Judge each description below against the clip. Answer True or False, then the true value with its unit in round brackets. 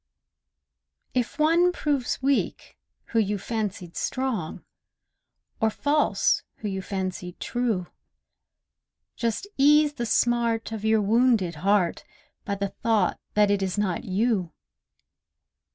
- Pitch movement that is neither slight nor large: True (4.2 semitones)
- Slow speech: True (115 wpm)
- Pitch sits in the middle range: False (220 Hz)